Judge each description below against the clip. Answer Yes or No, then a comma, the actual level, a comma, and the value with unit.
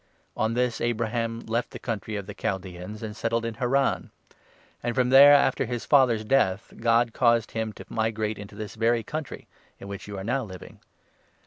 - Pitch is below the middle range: Yes, low, 115 Hz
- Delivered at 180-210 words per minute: Yes, average, 190 wpm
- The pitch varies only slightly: Yes, narrow, 2.2 semitones